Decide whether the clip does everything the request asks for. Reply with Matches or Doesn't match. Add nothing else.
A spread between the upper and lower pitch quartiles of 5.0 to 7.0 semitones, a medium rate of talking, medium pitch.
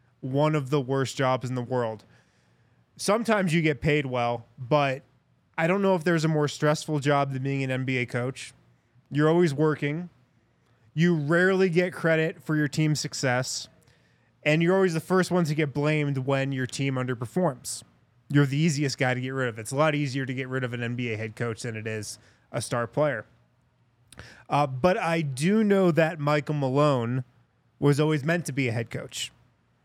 Doesn't match